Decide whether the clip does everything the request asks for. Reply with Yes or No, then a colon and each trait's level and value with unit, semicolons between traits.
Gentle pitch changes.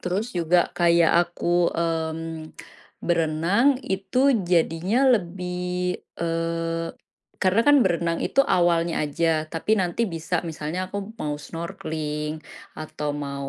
Yes: narrow, 1.7 semitones